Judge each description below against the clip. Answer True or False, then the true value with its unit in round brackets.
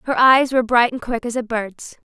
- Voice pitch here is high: True (240 Hz)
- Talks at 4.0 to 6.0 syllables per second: True (5.1 syllables/s)